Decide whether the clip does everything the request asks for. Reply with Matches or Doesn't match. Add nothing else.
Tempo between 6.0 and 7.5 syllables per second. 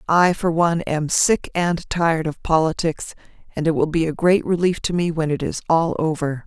Doesn't match